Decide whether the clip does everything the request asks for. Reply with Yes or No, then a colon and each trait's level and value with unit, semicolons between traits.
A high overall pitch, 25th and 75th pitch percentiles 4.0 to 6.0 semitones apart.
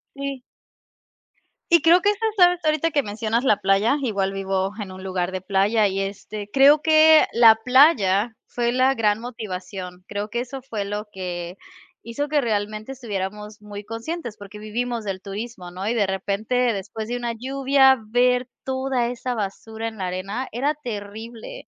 Yes: high, 220 Hz; average, 4.6 semitones